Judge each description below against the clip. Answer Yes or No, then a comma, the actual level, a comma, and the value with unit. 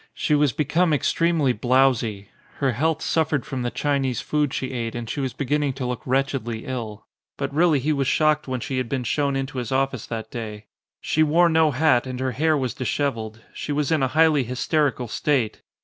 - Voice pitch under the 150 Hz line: Yes, low, 135 Hz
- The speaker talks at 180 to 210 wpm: Yes, fast, 205 wpm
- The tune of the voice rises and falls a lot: No, average, 3.3 semitones